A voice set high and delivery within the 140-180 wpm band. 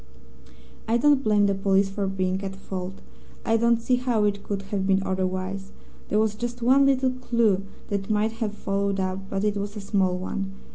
No: high, 200 Hz; average, 200 wpm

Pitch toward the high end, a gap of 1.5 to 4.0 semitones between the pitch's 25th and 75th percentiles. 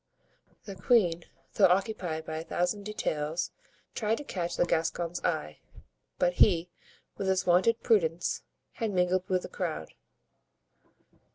No: medium, 180 Hz; average, 3.1 semitones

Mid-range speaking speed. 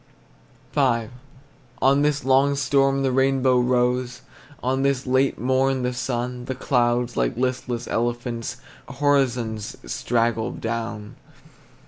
No: slow, 110 wpm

